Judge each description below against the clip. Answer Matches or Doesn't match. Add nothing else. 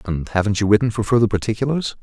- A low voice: Matches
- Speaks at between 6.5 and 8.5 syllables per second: Matches